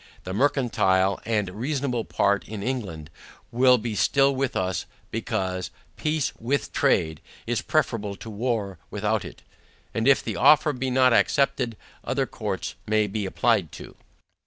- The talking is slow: No, average, 145 wpm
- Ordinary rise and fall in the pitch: Yes, average, 4.7 semitones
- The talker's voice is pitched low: Yes, low, 115 Hz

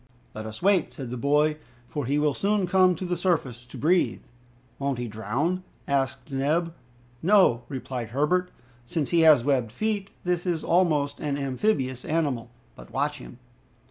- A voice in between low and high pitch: Yes, medium, 145 Hz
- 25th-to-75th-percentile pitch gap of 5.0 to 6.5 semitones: Yes, wide, 5.4 semitones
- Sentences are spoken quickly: No, average, 165 wpm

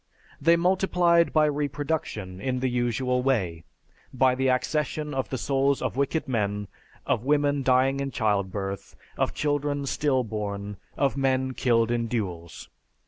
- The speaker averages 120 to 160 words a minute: Yes, average, 140 wpm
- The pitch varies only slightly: No, average, 4.6 semitones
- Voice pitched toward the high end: No, low, 130 Hz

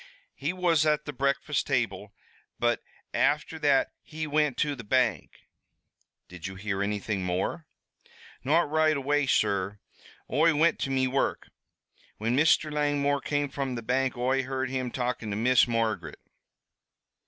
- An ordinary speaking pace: Yes, average, 145 wpm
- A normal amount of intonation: Yes, average, 4.4 semitones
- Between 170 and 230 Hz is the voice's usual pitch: No, low, 135 Hz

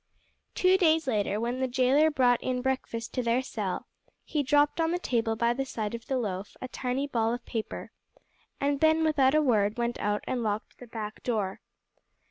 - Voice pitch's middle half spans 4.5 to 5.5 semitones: No, average, 3.9 semitones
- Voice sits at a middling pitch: No, very high, 250 Hz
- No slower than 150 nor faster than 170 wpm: No, average, 195 wpm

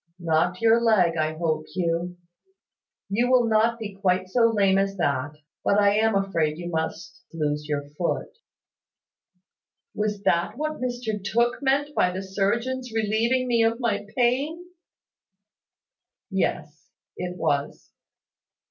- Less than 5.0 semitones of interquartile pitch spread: No, wide, 5.4 semitones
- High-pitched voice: Yes, high, 200 Hz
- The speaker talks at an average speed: No, slow, 130 wpm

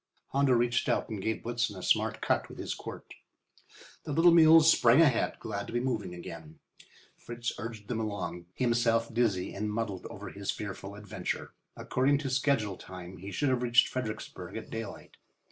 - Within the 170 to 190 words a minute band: Yes, average, 175 wpm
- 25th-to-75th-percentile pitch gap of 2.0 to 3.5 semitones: No, average, 3.9 semitones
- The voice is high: No, low, 115 Hz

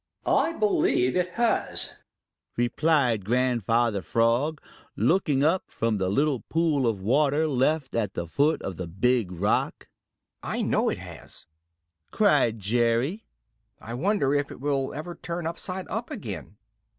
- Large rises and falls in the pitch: Yes, wide, 5.7 semitones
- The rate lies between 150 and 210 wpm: No, average, 140 wpm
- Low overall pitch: Yes, low, 130 Hz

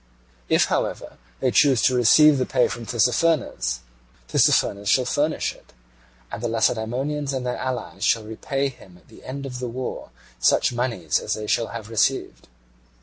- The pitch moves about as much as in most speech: Yes, average, 3.3 semitones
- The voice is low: Yes, low, 120 Hz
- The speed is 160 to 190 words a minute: Yes, average, 165 wpm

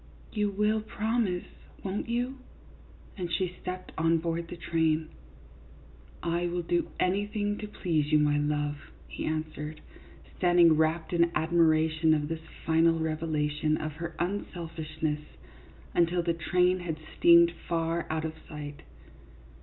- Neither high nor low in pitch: Yes, medium, 165 Hz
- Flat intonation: Yes, narrow, 2.2 semitones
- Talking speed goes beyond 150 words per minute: No, average, 140 wpm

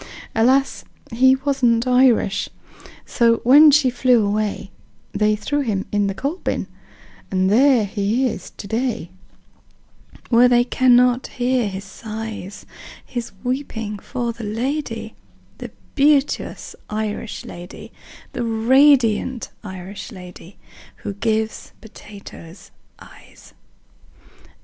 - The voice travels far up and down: No, average, 3.8 semitones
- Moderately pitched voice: No, high, 230 Hz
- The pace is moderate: No, slow, 110 wpm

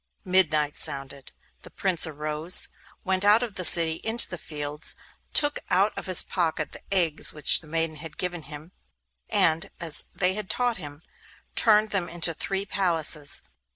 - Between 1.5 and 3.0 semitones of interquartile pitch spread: No, average, 3.7 semitones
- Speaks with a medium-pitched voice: Yes, medium, 170 Hz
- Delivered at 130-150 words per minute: No, average, 160 wpm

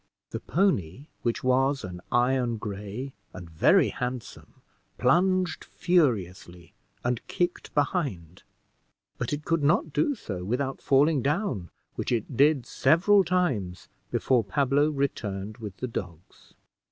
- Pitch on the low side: Yes, low, 130 Hz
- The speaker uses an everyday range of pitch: No, wide, 6.9 semitones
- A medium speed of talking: No, slow, 125 wpm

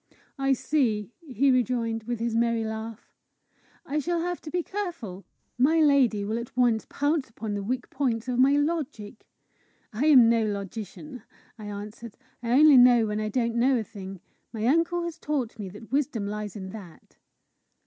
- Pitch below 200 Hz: No, high, 235 Hz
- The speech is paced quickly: No, average, 175 wpm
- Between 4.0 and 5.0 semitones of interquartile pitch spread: Yes, average, 4.6 semitones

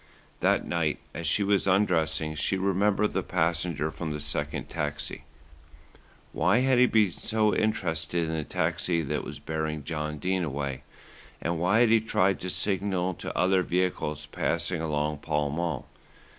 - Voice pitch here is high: No, very low, 85 Hz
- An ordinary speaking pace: Yes, average, 155 wpm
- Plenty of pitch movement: No, average, 3.9 semitones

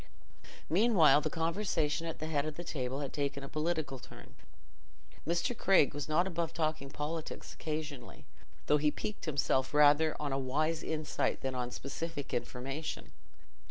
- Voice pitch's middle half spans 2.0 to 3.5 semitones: Yes, average, 2.7 semitones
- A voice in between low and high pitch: Yes, medium, 155 Hz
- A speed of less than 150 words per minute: No, average, 155 wpm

